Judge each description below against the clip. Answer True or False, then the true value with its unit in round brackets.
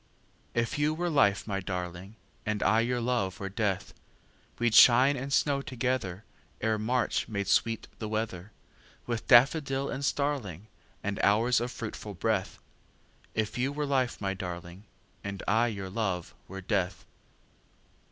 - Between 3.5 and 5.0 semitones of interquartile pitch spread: True (4.4 semitones)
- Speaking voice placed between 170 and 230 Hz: False (110 Hz)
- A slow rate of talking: True (125 wpm)